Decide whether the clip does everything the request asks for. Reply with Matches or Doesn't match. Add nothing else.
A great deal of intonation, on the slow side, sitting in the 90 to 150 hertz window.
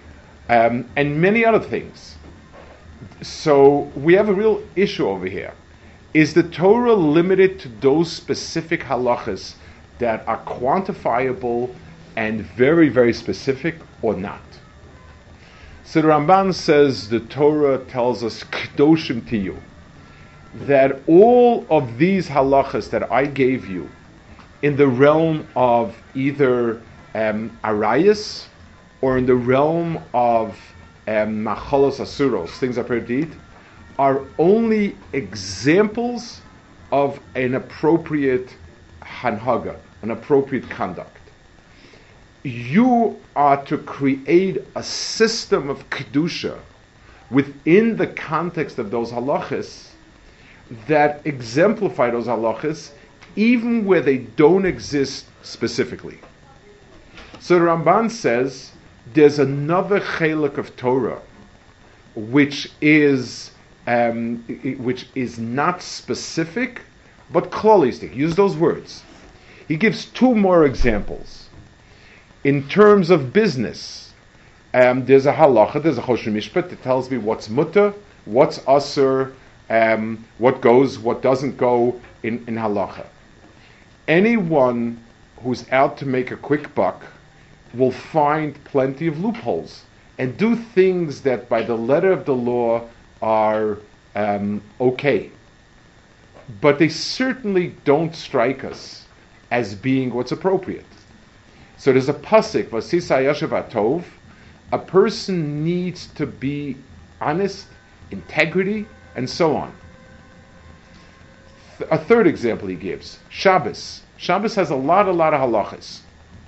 Matches